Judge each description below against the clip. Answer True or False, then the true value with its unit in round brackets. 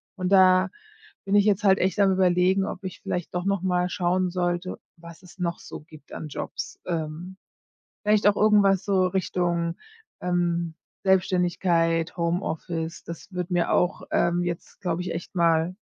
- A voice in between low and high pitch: True (180 Hz)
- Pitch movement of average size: False (1.9 semitones)